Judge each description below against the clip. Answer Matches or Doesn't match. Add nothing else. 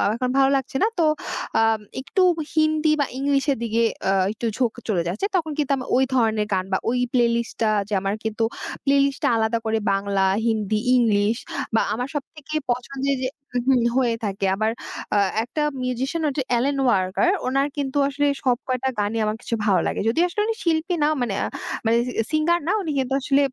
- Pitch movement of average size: Matches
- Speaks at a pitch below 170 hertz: Doesn't match